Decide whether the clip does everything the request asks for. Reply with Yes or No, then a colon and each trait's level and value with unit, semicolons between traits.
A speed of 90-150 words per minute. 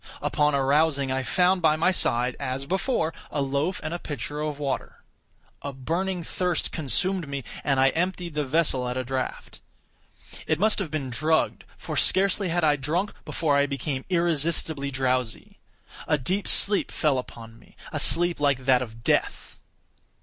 No: average, 160 wpm